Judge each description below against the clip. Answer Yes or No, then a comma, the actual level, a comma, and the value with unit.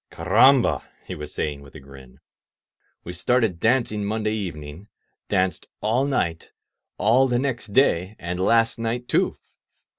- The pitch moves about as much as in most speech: No, wide, 6.1 semitones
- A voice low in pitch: Yes, low, 105 Hz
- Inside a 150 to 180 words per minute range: No, average, 140 wpm